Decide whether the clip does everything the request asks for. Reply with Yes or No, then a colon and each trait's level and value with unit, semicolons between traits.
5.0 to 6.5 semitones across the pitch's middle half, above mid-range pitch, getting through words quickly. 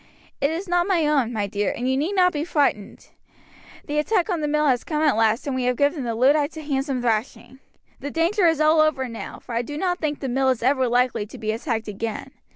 No: average, 4.3 semitones; very high, 280 Hz; fast, 245 wpm